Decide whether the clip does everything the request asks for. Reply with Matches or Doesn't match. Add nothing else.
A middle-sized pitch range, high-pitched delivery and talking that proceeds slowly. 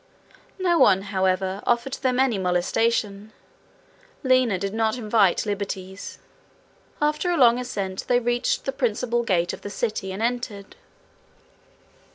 Matches